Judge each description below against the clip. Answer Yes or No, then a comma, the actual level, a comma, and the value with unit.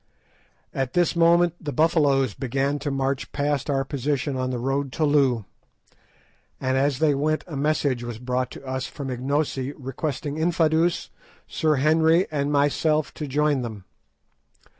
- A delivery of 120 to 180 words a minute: Yes, average, 150 wpm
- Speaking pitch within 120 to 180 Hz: Yes, medium, 140 Hz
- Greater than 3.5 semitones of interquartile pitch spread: No, average, 2.7 semitones